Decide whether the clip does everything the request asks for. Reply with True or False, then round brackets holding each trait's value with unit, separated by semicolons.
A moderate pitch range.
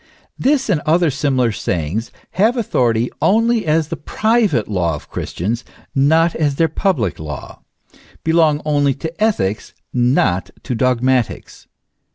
False (6.5 semitones)